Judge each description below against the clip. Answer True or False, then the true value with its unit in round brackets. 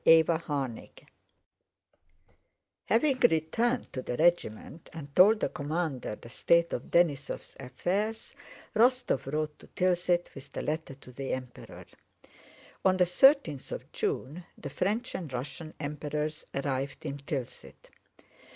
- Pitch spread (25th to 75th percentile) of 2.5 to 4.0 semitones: False (4.6 semitones)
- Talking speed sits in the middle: False (125 wpm)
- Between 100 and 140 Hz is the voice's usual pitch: False (155 Hz)